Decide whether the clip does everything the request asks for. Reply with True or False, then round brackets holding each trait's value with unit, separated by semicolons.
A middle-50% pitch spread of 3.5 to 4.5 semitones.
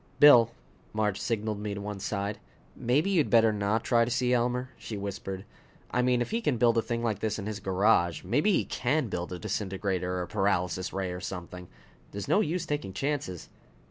True (4.2 semitones)